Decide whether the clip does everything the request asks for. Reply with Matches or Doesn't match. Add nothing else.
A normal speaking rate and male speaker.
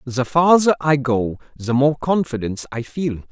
Matches